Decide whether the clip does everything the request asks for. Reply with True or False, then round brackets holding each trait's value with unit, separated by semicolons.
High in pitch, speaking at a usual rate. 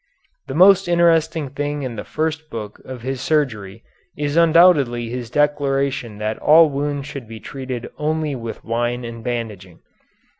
False (135 Hz; 150 wpm)